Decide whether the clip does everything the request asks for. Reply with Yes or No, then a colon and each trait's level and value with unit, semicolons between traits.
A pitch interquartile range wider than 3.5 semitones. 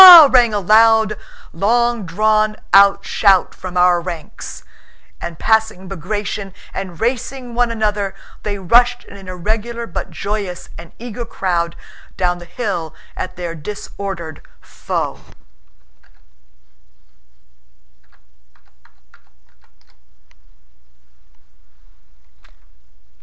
Yes: average, 4.2 semitones